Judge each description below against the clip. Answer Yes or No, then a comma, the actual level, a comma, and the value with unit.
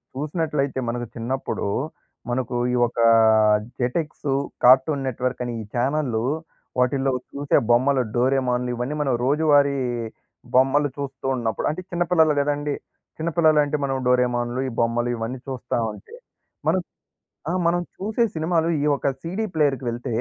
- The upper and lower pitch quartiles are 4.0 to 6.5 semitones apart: No, average, 3.4 semitones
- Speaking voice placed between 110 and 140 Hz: Yes, low, 135 Hz